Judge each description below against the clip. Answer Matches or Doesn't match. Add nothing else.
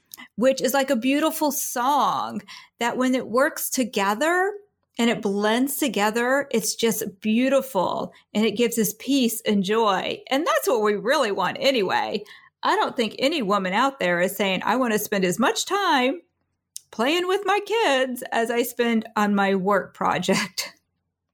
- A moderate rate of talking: Matches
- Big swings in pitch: Doesn't match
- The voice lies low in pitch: Doesn't match